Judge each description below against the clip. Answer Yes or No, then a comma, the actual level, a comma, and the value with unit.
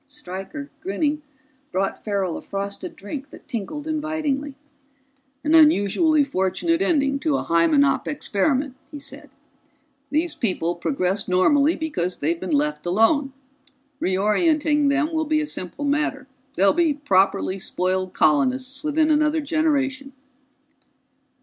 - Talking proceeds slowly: Yes, slow, 125 wpm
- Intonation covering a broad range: Yes, wide, 7.5 semitones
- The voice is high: Yes, very high, 280 Hz